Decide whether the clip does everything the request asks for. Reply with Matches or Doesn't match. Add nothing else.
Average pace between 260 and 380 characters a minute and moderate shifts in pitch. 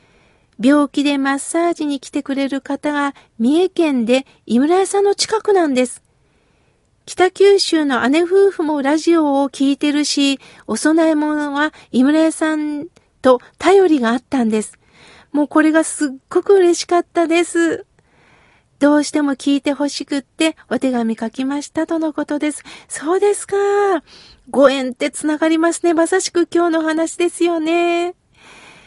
Matches